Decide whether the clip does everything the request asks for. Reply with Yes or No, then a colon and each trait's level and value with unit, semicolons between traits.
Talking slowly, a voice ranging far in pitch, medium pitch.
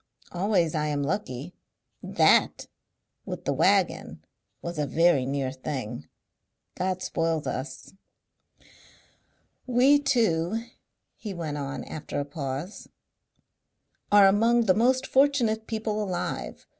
Yes: slow, 110 wpm; wide, 7.0 semitones; medium, 175 Hz